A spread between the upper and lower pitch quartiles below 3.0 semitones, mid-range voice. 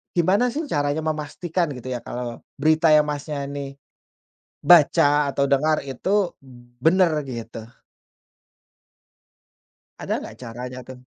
No: average, 4.0 semitones; medium, 145 Hz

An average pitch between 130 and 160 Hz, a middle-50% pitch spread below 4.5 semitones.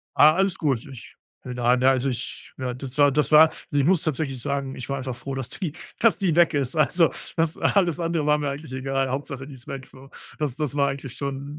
Yes: medium, 140 Hz; average, 2.7 semitones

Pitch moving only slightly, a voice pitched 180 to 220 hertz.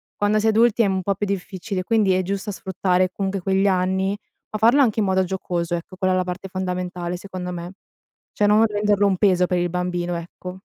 Yes: narrow, 2.1 semitones; high, 190 Hz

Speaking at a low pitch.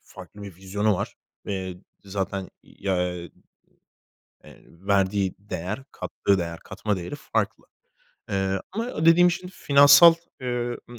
Yes: low, 100 Hz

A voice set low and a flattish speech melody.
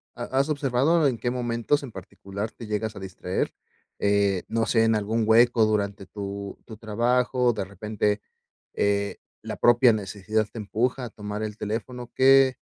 No: low, 110 Hz; average, 3.1 semitones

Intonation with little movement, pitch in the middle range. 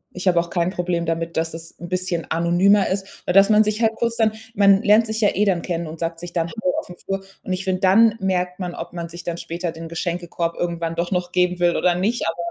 Yes: narrow, 2.3 semitones; medium, 180 Hz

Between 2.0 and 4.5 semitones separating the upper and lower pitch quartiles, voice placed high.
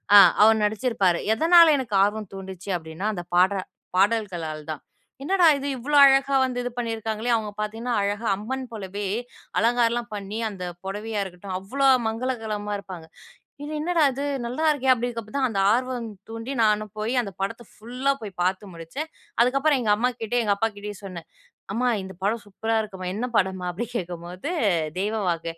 Yes: average, 4.2 semitones; high, 220 Hz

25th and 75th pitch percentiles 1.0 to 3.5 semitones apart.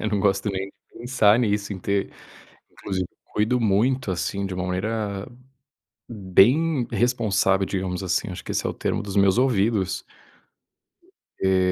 Yes: average, 3.0 semitones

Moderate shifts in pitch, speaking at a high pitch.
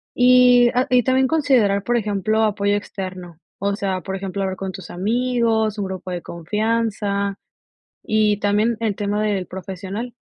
Yes: average, 3.1 semitones; high, 205 Hz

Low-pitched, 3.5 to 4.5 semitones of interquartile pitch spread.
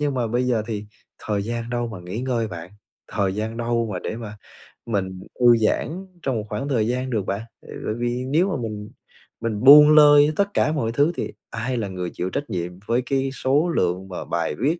Yes: low, 115 Hz; average, 4.2 semitones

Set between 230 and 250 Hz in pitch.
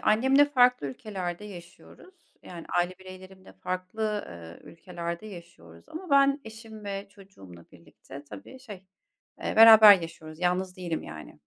No: medium, 185 Hz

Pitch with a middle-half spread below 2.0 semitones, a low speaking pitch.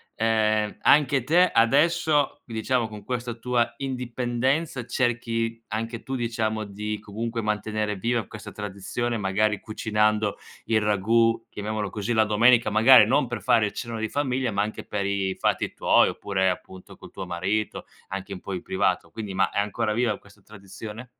No: narrow, 2.5 semitones; low, 110 Hz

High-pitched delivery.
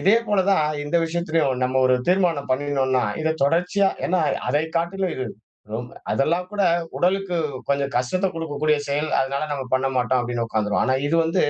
No: medium, 150 Hz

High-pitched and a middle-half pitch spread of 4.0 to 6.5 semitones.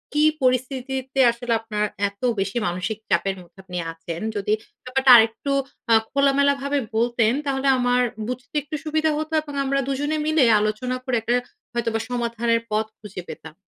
Yes: high, 245 Hz; average, 4.4 semitones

